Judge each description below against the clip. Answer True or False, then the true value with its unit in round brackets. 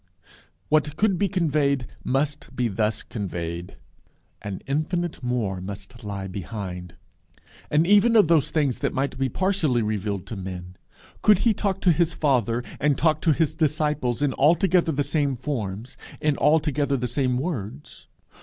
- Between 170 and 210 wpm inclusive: False (155 wpm)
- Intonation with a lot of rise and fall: True (6.6 semitones)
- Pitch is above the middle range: False (135 Hz)